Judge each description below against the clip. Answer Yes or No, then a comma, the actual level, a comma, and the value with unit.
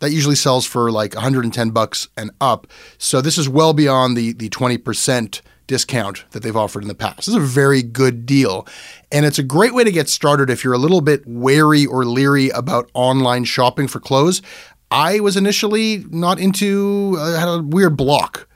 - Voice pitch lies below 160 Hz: Yes, low, 135 Hz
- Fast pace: No, average, 195 wpm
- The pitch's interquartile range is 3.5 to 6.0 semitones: Yes, average, 5.0 semitones